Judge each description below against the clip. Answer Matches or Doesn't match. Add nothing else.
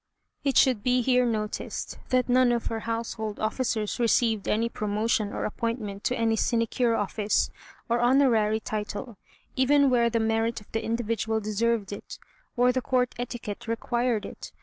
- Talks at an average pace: Matches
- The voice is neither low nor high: Doesn't match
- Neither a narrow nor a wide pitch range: Doesn't match